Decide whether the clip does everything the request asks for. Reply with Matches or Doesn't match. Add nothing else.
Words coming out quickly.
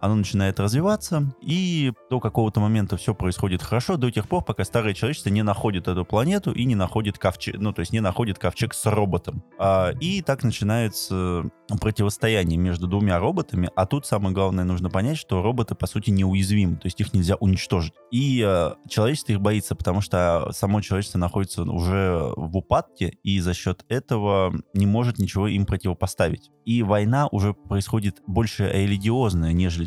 Matches